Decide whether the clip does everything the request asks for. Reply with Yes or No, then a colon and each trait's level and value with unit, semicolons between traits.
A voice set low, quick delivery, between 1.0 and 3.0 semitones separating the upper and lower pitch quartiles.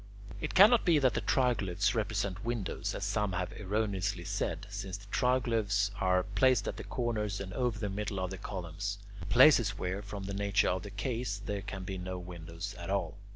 No: low, 100 Hz; average, 190 wpm; narrow, 2.6 semitones